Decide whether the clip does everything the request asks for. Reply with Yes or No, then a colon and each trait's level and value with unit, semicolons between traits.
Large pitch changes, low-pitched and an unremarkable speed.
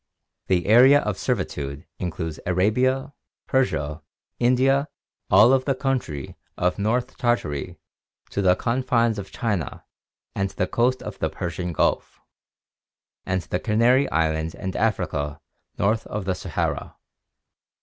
No: wide, 6.2 semitones; low, 105 Hz; slow, 125 wpm